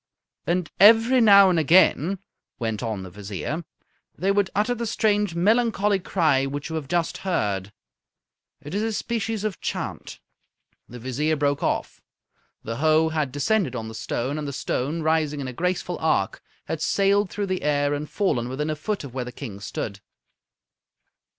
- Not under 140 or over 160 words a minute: No, average, 170 wpm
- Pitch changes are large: Yes, wide, 7.0 semitones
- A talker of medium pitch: Yes, medium, 155 Hz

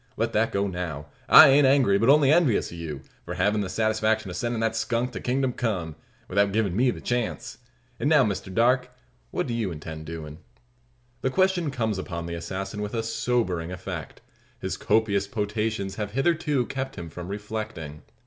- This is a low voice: Yes, low, 110 Hz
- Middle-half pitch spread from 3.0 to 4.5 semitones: No, average, 4.9 semitones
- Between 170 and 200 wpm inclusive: Yes, average, 185 wpm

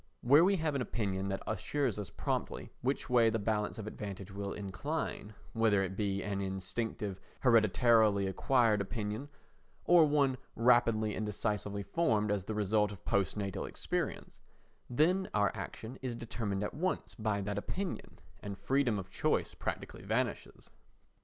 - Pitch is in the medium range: No, low, 105 Hz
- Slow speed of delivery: No, average, 145 wpm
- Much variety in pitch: No, average, 3.7 semitones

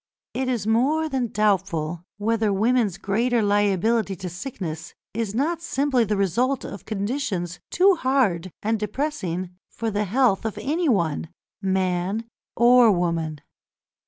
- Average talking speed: No, slow, 130 wpm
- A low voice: No, high, 210 Hz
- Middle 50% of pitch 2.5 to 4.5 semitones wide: No, average, 5.1 semitones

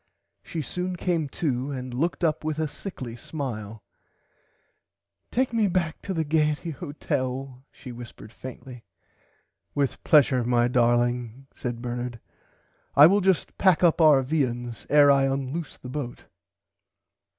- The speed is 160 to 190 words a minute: No, slow, 135 wpm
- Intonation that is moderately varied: Yes, average, 4.5 semitones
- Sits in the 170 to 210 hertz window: No, low, 135 Hz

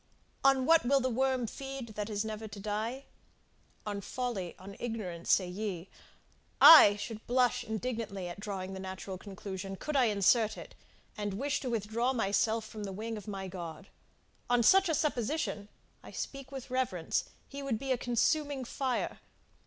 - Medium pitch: No, high, 220 Hz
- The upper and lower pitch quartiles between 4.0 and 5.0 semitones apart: Yes, average, 4.4 semitones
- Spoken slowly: No, average, 170 wpm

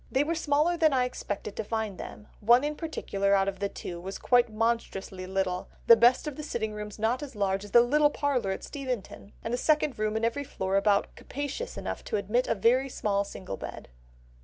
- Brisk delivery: Yes, fast, 215 wpm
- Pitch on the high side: Yes, high, 230 Hz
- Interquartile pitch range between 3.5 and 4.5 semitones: No, average, 5.3 semitones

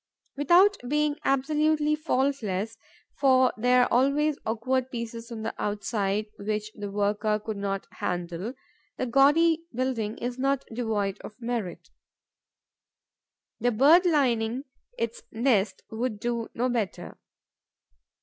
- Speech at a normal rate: No, slow, 120 wpm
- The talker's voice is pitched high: Yes, high, 240 Hz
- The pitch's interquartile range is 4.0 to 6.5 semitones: Yes, average, 4.3 semitones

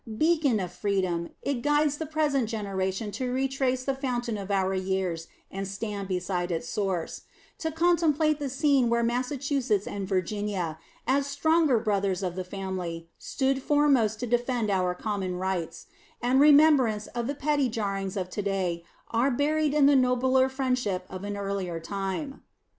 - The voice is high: Yes, high, 225 Hz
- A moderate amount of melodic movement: No, wide, 6.2 semitones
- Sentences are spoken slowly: No, average, 160 wpm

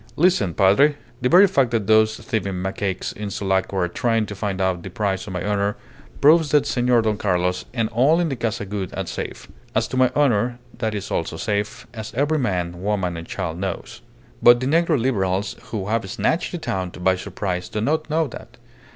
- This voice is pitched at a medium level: No, low, 105 Hz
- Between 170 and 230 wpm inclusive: Yes, fast, 205 wpm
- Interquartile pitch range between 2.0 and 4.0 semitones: No, average, 4.9 semitones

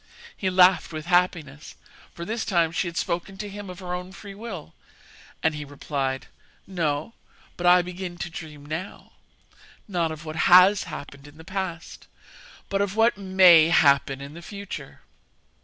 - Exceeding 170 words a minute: No, average, 165 wpm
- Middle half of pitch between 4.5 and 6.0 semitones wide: No, average, 3.4 semitones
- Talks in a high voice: No, medium, 175 Hz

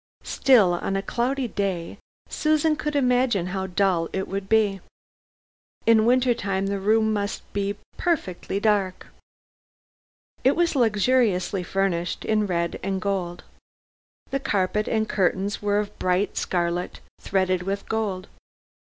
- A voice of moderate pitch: No, high, 200 Hz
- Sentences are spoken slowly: Yes, slow, 130 wpm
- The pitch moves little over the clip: No, average, 3.1 semitones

